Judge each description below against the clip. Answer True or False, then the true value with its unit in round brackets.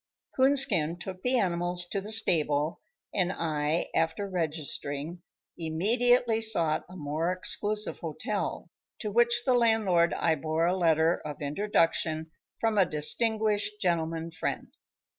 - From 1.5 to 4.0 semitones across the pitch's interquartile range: False (5.0 semitones)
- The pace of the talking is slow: True (120 wpm)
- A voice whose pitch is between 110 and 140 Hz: False (175 Hz)